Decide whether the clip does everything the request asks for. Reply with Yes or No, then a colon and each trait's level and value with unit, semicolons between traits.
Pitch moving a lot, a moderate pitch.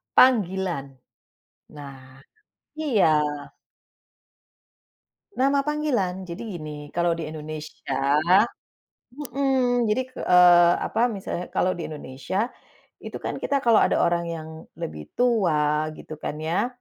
Yes: wide, 7.8 semitones; medium, 180 Hz